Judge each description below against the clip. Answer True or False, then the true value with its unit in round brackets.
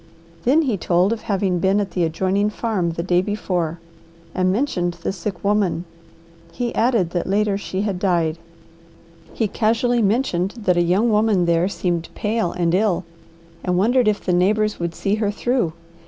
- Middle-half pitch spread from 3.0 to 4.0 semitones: True (3.4 semitones)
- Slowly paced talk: False (170 wpm)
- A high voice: True (195 Hz)